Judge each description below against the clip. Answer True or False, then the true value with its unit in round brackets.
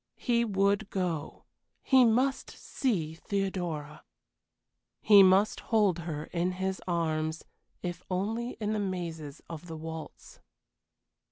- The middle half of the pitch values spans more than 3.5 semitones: True (4.2 semitones)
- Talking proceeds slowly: True (115 wpm)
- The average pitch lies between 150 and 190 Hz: True (185 Hz)